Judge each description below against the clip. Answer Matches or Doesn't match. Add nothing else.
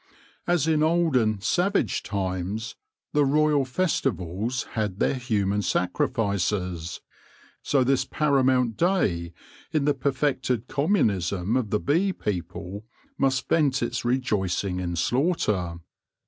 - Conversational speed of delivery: Doesn't match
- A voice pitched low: Matches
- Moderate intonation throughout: Doesn't match